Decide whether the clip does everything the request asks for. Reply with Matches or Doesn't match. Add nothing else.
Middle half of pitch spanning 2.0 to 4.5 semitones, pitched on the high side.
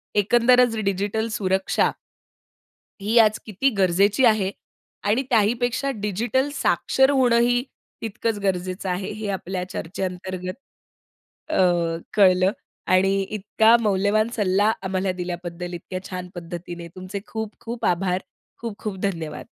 Matches